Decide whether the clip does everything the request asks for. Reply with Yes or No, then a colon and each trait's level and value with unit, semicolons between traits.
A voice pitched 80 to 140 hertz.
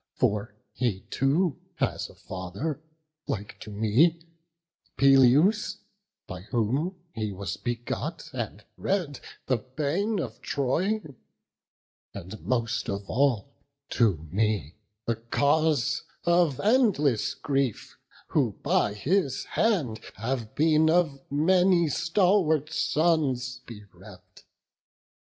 Yes: low, 135 Hz